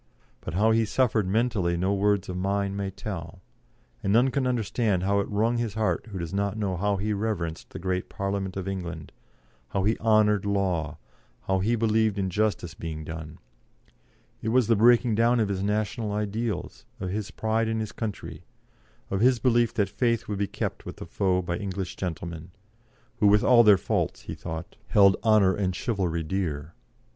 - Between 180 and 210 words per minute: Yes, average, 185 wpm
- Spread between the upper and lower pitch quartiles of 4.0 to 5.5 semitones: No, average, 3.1 semitones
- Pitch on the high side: No, low, 100 Hz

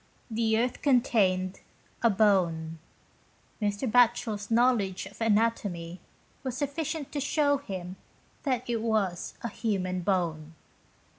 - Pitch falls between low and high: No, high, 215 Hz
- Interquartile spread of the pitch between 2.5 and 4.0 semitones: No, average, 4.7 semitones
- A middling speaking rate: No, slow, 120 wpm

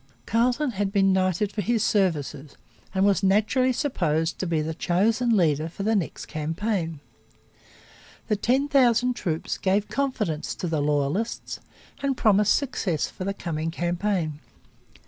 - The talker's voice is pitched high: Yes, high, 195 Hz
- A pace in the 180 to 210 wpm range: No, average, 145 wpm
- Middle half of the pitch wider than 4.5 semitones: Yes, wide, 5.6 semitones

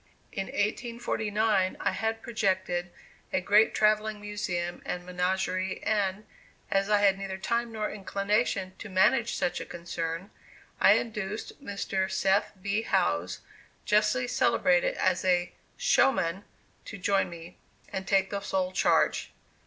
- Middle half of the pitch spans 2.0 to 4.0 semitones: Yes, narrow, 2.5 semitones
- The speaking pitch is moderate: No, high, 195 Hz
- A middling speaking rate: No, slow, 130 wpm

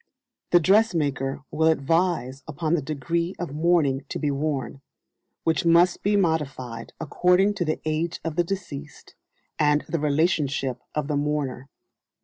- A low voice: No, medium, 155 Hz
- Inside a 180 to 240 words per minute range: No, average, 140 wpm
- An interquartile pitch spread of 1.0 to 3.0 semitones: No, average, 3.5 semitones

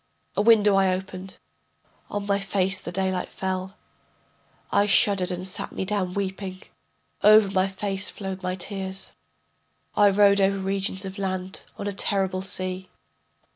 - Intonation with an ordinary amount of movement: No, narrow, 1.1 semitones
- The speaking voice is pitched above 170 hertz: Yes, high, 190 Hz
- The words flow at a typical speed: Yes, average, 145 wpm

